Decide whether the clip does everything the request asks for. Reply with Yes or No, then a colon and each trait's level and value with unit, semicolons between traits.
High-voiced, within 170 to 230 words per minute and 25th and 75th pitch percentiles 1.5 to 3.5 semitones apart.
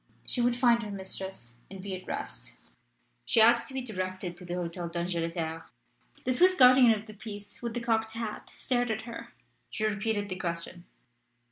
No: high, 205 Hz; average, 180 wpm; average, 4.4 semitones